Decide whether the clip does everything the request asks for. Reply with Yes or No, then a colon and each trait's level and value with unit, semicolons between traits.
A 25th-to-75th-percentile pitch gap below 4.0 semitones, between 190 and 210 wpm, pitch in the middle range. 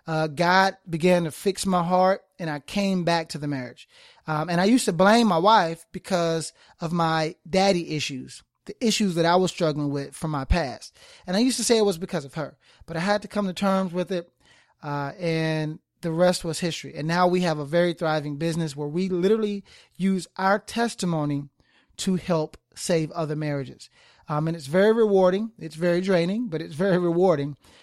Yes: average, 3.3 semitones; average, 200 wpm; medium, 175 Hz